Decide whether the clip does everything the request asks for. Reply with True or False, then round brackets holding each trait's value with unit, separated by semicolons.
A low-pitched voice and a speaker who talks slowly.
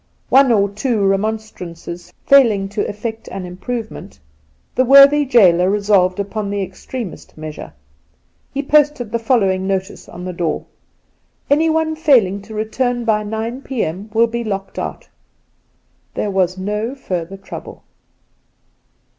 False (210 Hz; 130 wpm)